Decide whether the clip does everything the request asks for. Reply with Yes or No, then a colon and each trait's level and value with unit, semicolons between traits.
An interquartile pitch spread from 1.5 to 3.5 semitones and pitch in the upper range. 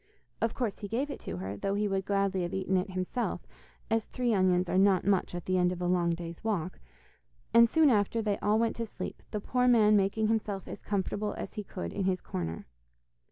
Yes: average, 3.2 semitones; high, 200 Hz